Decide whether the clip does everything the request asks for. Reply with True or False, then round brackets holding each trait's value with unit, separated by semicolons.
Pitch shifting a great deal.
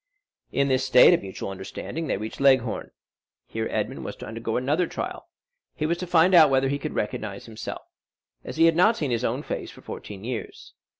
True (5.9 semitones)